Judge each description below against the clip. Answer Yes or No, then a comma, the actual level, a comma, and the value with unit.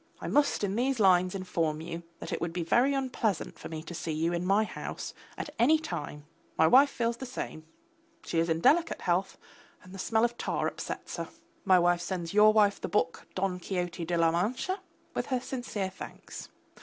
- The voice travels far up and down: Yes, wide, 5.8 semitones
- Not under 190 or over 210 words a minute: Yes, fast, 205 wpm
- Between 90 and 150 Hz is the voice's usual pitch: No, high, 190 Hz